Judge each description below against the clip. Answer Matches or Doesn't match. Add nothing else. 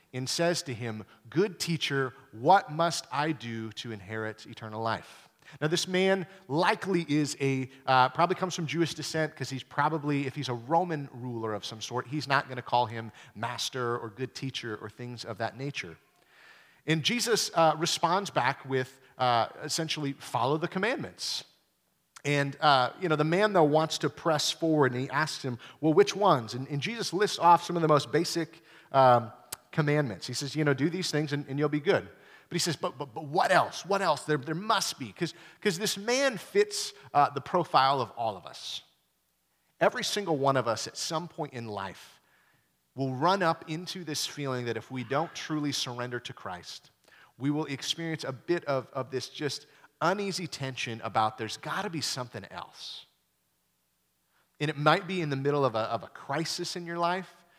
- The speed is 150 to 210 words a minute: Matches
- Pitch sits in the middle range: Matches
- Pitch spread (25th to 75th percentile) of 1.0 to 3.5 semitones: Doesn't match